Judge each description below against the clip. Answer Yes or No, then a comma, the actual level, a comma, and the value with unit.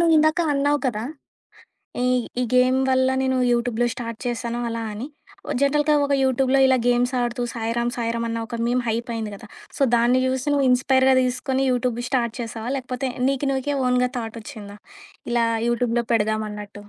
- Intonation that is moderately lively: No, narrow, 2.2 semitones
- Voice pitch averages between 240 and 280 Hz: Yes, high, 245 Hz